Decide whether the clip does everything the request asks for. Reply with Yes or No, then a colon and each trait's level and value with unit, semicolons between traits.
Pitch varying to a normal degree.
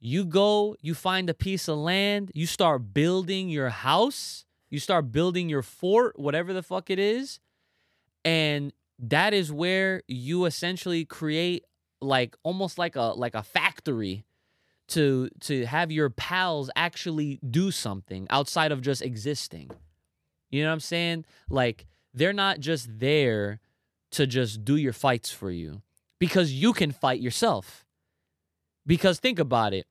No: wide, 6.9 semitones